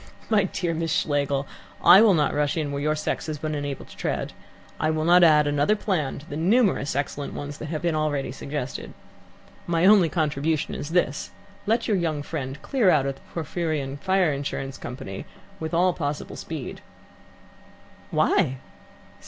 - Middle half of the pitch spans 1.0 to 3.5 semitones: Yes, average, 3.2 semitones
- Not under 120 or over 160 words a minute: No, average, 170 wpm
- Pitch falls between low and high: Yes, medium, 155 Hz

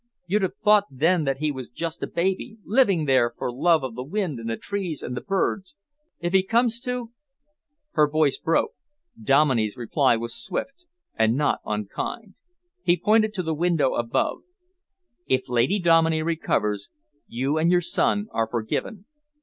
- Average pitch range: No, wide, 7.3 semitones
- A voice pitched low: No, medium, 160 Hz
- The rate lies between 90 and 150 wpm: No, average, 165 wpm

